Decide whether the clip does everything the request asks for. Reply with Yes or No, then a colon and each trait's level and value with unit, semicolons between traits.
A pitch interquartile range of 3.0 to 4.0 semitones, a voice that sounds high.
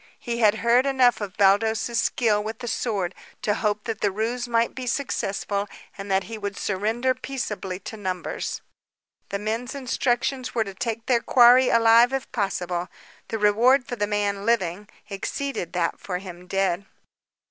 Yes: average, 3.4 semitones; high, 220 Hz